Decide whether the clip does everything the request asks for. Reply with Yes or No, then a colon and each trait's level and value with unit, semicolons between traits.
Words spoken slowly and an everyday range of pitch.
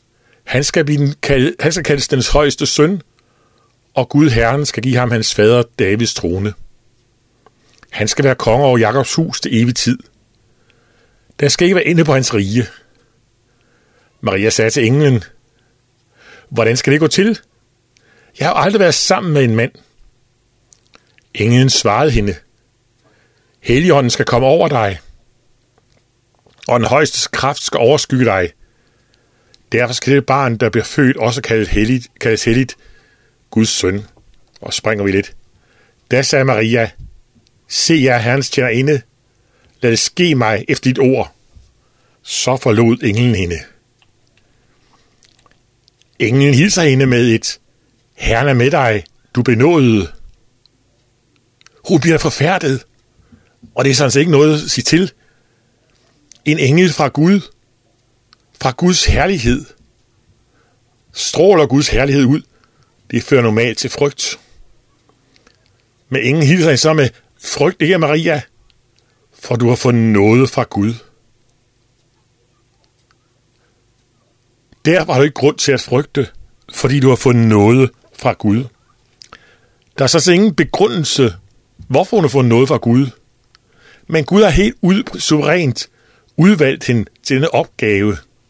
Yes: slow, 135 wpm; average, 3.2 semitones